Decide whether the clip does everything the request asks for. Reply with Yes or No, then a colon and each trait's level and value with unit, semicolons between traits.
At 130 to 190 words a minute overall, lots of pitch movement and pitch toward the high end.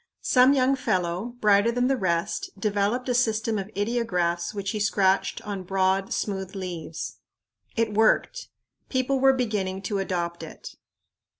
No: average, 140 wpm; average, 4.1 semitones; high, 205 Hz